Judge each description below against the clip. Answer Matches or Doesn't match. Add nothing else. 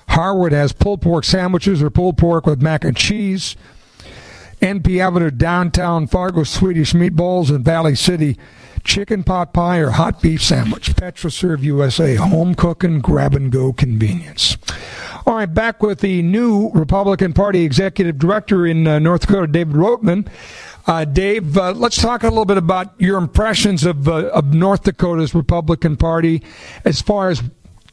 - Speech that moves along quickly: Doesn't match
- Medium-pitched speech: Matches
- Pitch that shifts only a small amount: Doesn't match